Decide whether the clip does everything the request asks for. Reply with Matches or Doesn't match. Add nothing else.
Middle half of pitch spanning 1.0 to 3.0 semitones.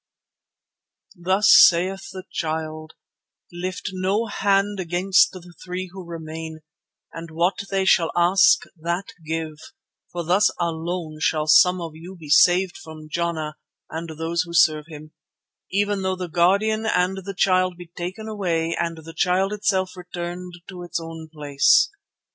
Matches